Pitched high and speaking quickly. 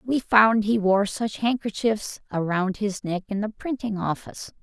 No: high, 210 Hz; average, 170 wpm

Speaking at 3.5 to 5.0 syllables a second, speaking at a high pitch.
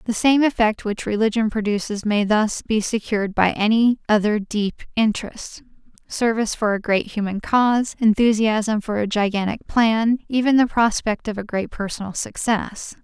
Yes: 4.9 syllables/s; high, 220 Hz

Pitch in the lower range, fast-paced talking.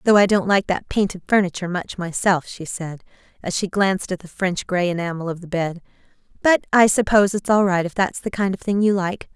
No: high, 190 Hz; fast, 230 wpm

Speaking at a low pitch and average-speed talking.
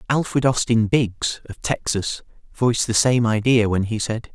Yes: low, 115 Hz; average, 165 wpm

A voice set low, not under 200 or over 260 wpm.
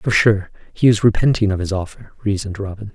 Yes: low, 100 Hz; fast, 205 wpm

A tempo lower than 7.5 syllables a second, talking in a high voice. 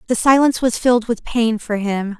Yes: 5.5 syllables/s; high, 230 Hz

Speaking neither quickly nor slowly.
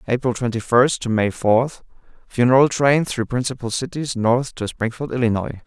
Yes: average, 160 wpm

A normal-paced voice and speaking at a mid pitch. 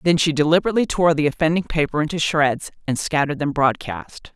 Yes: average, 180 wpm; medium, 155 Hz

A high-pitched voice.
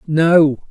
No: medium, 155 Hz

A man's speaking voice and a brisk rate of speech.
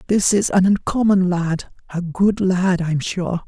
No: male; average, 175 wpm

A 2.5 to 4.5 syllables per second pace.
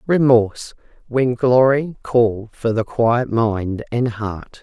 Yes: 3.5 syllables/s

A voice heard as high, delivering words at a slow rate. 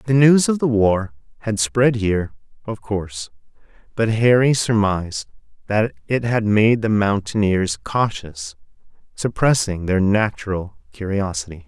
No: low, 105 Hz; slow, 125 wpm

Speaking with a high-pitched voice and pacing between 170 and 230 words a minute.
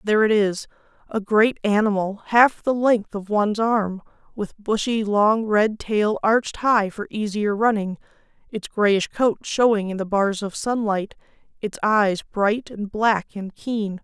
No: high, 210 Hz; average, 160 wpm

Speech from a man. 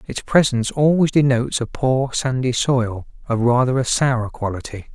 Yes: male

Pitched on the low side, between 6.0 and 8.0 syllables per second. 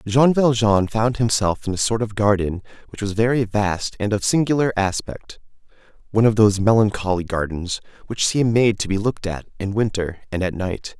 No: low, 105 Hz; 5.3 syllables/s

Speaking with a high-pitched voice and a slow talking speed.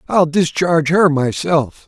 No: medium, 160 Hz; slow, 130 wpm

